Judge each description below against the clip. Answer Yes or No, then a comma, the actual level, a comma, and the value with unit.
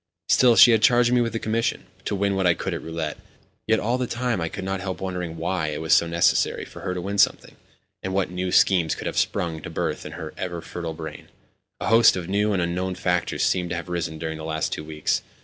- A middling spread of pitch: Yes, average, 3.5 semitones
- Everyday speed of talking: No, fast, 245 wpm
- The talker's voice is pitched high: No, very low, 90 Hz